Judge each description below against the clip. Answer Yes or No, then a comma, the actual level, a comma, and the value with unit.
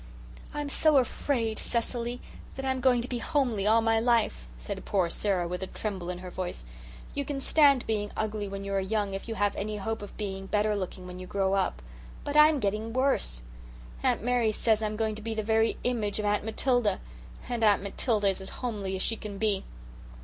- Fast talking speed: Yes, fast, 210 wpm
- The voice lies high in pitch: Yes, high, 215 Hz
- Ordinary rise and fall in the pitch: Yes, average, 3.4 semitones